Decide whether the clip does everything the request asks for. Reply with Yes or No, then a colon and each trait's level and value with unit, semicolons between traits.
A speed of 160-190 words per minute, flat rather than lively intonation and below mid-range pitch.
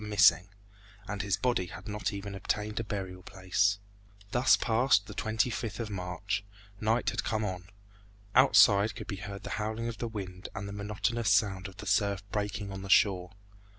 Yes: average, 180 wpm; narrow, 2.1 semitones; low, 105 Hz